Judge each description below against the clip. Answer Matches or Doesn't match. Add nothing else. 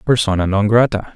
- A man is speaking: Matches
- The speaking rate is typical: Matches